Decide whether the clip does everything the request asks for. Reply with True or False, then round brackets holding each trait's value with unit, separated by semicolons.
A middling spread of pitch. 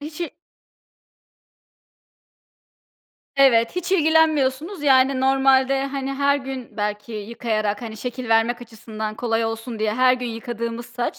True (3.3 semitones)